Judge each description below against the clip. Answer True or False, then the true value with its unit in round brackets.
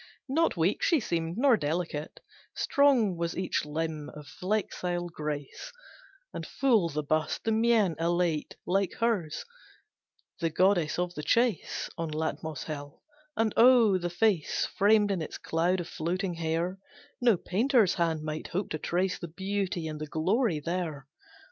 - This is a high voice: False (175 Hz)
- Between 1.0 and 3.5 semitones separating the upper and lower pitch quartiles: False (4.4 semitones)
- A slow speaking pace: False (150 wpm)